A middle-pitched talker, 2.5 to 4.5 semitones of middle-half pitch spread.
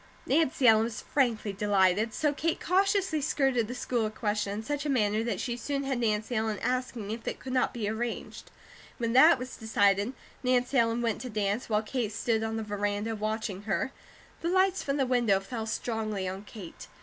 No: high, 230 Hz; average, 3.4 semitones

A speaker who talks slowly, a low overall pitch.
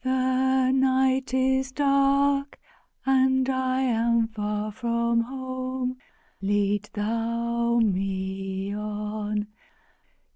No: slow, 80 wpm; high, 235 Hz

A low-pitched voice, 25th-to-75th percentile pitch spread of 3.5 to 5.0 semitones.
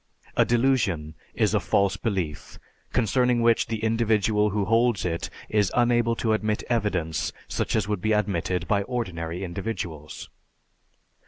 Yes: low, 105 Hz; average, 4.2 semitones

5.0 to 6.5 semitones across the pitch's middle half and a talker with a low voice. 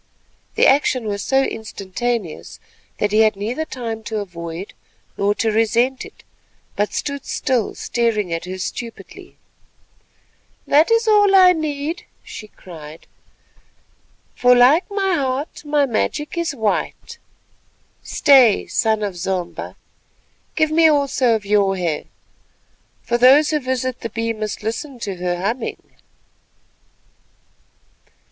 No: wide, 5.6 semitones; high, 235 Hz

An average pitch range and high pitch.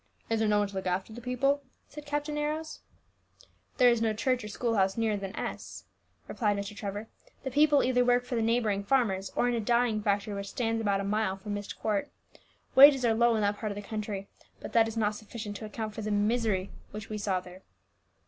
Yes: average, 3.1 semitones; high, 220 Hz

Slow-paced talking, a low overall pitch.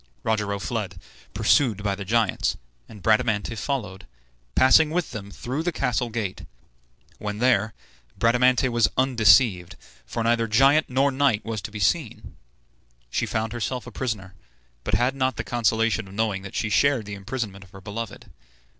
No: average, 160 wpm; low, 115 Hz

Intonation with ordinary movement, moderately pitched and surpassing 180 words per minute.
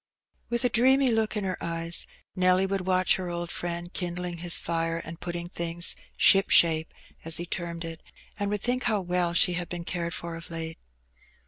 No: narrow, 2.0 semitones; medium, 175 Hz; average, 200 wpm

